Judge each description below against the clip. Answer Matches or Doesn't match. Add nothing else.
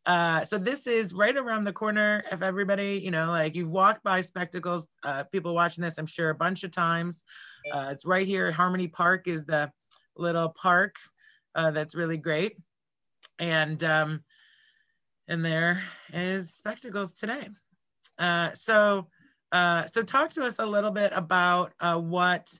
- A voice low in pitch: Doesn't match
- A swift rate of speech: Doesn't match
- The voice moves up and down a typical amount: Matches